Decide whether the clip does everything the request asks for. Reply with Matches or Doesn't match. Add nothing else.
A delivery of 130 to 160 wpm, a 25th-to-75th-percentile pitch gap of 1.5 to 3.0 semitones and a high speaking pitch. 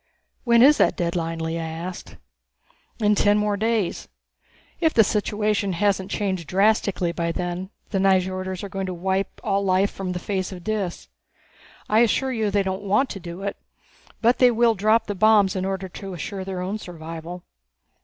Doesn't match